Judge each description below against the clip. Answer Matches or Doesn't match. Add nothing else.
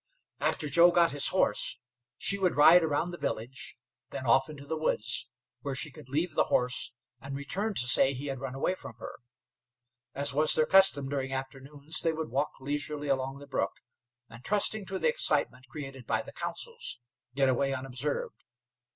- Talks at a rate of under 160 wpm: Doesn't match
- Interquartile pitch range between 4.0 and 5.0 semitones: Doesn't match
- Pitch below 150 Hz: Matches